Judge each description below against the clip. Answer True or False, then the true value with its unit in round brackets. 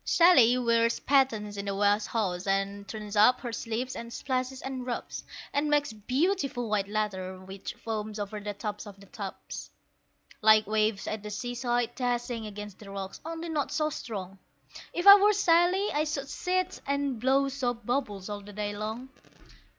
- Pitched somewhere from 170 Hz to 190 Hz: False (230 Hz)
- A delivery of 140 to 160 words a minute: False (175 wpm)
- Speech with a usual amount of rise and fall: True (4.7 semitones)